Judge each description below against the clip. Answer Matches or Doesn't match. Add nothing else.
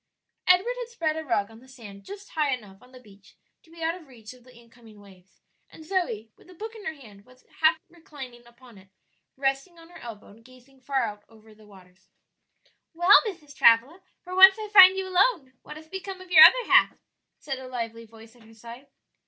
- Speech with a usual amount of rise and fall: Doesn't match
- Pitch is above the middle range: Matches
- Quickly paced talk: Matches